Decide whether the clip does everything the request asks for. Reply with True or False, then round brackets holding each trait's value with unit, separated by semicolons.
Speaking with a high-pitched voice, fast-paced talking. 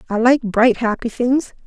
False (240 Hz; 180 wpm)